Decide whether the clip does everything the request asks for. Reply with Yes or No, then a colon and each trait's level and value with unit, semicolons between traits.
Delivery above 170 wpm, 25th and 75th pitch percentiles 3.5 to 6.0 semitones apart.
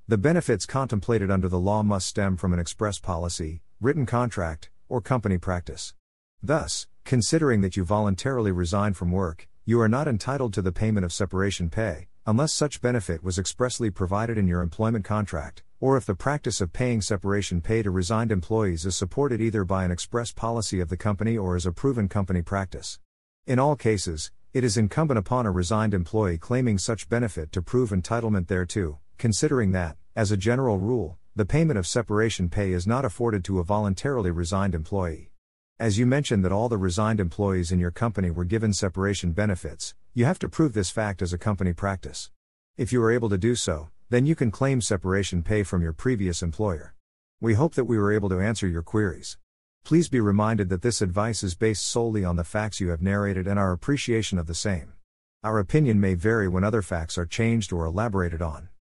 Yes: average, 195 wpm; average, 4.1 semitones